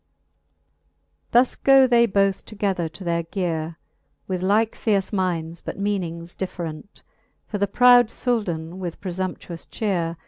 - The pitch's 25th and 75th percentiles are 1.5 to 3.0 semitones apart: No, average, 3.8 semitones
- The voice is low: No, high, 190 Hz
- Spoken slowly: Yes, slow, 130 wpm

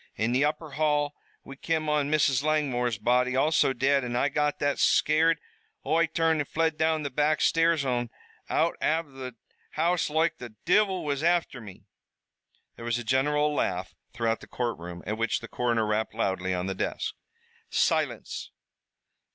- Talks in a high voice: No, medium, 140 Hz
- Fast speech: No, average, 165 wpm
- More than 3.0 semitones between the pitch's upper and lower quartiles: Yes, average, 4.5 semitones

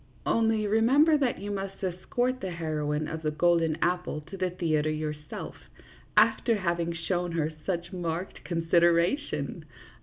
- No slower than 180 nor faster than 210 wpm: No, average, 140 wpm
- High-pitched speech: No, medium, 175 Hz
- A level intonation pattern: No, average, 3.4 semitones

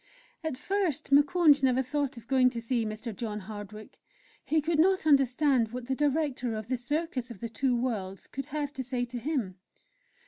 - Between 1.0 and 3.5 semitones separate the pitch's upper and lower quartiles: No, average, 4.1 semitones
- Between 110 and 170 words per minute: No, average, 185 wpm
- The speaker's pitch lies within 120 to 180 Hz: No, very high, 255 Hz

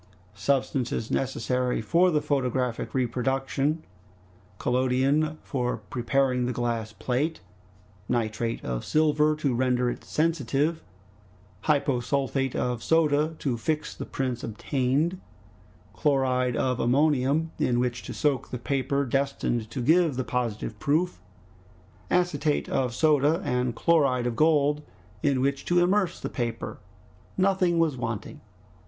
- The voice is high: No, low, 135 Hz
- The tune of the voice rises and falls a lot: No, average, 3.6 semitones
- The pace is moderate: No, slow, 120 wpm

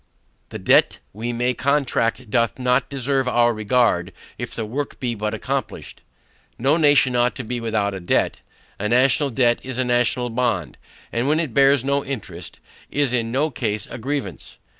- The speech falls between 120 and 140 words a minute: No, average, 175 wpm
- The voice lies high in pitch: No, low, 125 Hz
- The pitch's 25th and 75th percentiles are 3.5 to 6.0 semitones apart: No, average, 3.0 semitones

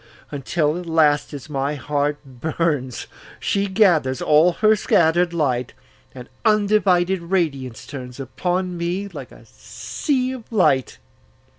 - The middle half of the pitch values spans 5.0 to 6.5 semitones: Yes, average, 5.3 semitones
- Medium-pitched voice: Yes, medium, 160 Hz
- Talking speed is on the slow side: Yes, slow, 110 wpm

